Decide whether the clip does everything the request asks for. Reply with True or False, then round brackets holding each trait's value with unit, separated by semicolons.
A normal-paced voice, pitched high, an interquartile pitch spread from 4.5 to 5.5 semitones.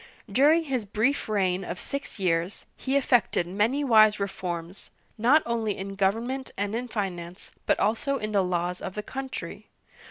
True (160 wpm; 210 Hz; 5.2 semitones)